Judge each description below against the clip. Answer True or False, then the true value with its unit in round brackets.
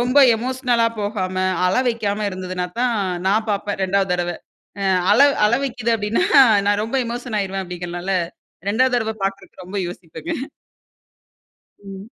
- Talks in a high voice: True (205 Hz)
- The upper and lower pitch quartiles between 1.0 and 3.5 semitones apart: False (3.9 semitones)